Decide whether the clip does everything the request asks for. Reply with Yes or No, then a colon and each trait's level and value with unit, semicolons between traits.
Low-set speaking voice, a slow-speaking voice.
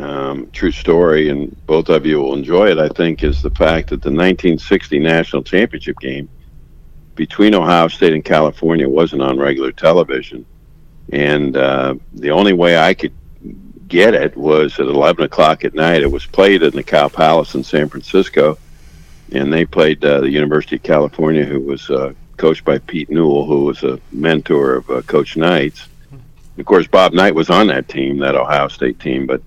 No: very low, 75 Hz; average, 185 wpm